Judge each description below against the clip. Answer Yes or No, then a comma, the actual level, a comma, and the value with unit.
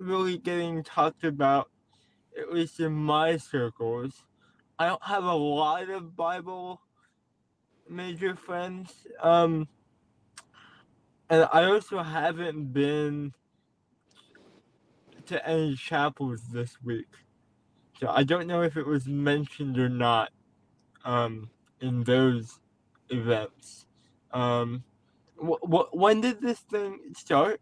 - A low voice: No, medium, 150 Hz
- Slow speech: Yes, slow, 110 wpm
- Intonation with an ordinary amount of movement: No, wide, 5.7 semitones